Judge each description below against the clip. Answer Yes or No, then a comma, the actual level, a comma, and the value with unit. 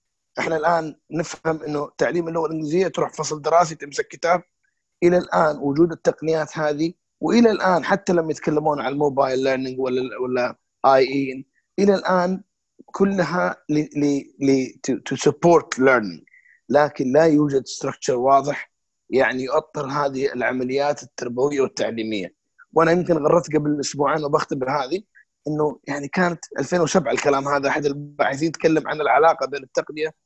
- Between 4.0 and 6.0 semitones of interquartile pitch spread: No, average, 3.4 semitones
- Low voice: No, medium, 150 Hz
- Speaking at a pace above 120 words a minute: Yes, average, 130 wpm